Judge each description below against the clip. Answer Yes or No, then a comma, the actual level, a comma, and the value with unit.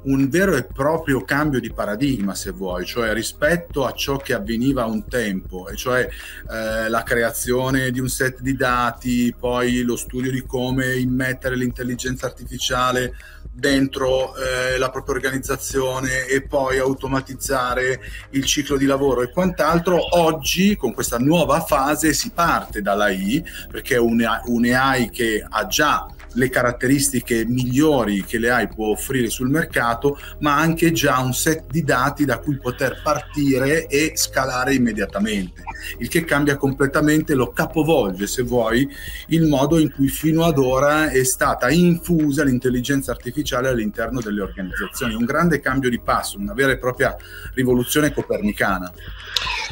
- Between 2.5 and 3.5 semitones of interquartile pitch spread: Yes, average, 2.9 semitones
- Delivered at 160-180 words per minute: No, average, 150 wpm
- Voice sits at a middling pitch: No, low, 130 Hz